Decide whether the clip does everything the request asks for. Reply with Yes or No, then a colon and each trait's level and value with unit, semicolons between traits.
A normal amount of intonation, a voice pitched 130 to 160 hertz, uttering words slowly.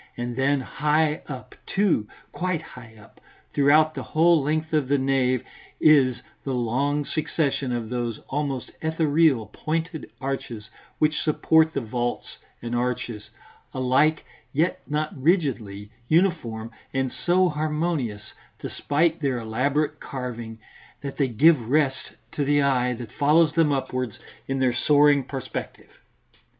Yes: average, 3.8 semitones; medium, 140 Hz; slow, 130 wpm